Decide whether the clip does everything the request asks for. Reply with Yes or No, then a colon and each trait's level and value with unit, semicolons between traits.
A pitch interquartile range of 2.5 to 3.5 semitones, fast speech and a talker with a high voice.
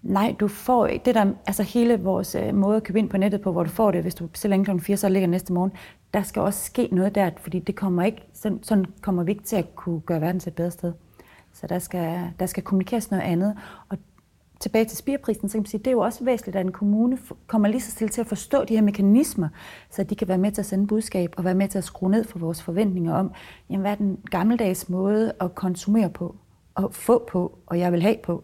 Yes: average, 2.9 semitones; fast, 265 wpm; high, 195 Hz